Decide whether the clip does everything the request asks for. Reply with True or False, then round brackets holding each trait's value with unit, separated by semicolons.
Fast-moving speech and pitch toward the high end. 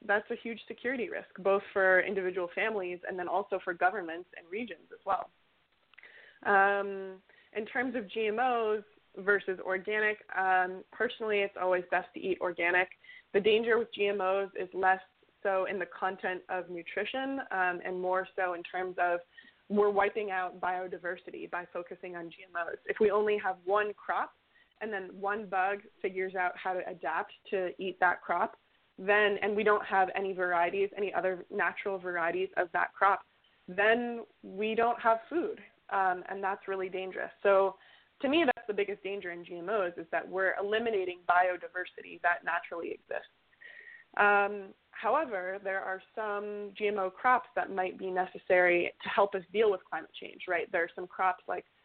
False (165 wpm; 195 Hz)